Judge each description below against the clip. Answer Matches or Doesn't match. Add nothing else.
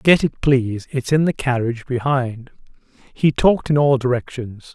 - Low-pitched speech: Matches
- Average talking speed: Matches